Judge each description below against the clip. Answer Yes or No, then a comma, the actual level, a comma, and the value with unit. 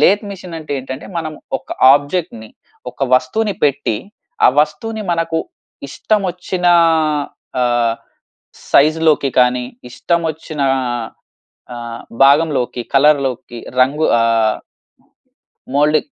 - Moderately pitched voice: Yes, medium, 145 Hz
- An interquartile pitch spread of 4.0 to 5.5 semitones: Yes, average, 4.6 semitones